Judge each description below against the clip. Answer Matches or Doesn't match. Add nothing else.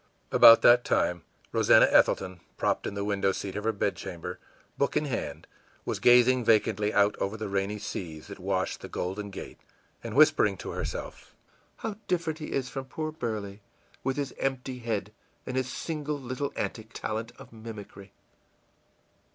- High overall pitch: Doesn't match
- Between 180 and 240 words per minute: Doesn't match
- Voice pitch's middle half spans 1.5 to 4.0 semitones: Doesn't match